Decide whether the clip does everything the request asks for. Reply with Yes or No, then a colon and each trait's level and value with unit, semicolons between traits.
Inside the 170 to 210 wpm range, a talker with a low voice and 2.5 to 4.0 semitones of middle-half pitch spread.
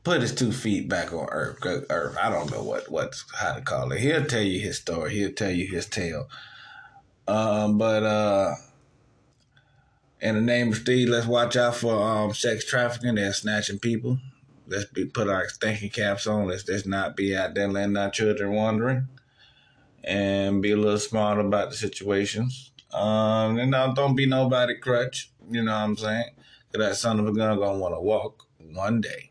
Yes: average, 190 wpm; low, 110 Hz; average, 3.5 semitones